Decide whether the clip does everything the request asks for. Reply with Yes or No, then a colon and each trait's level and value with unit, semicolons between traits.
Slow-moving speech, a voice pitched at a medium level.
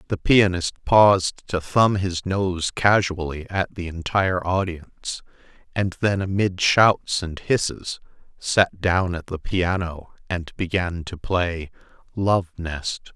No: slow, 130 wpm; very low, 90 Hz